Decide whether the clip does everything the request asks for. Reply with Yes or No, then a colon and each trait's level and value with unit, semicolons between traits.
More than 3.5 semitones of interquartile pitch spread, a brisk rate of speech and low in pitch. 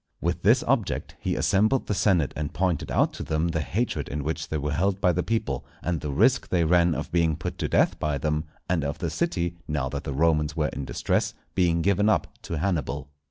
No: average, 3.2 semitones; fast, 225 wpm; very low, 80 Hz